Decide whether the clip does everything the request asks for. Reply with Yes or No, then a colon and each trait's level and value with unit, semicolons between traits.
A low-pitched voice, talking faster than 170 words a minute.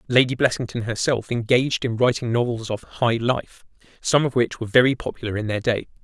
Yes: low, 120 Hz; average, 190 wpm